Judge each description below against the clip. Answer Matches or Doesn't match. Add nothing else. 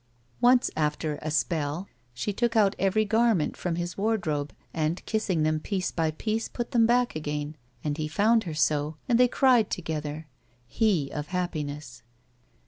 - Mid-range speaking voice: Matches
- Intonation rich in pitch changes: Matches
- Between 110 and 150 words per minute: Doesn't match